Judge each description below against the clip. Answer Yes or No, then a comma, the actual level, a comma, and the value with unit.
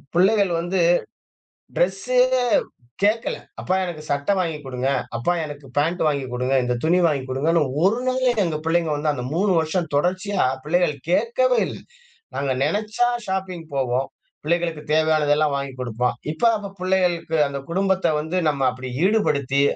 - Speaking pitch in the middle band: Yes, medium, 165 Hz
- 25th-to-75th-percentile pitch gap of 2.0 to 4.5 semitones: No, average, 5.0 semitones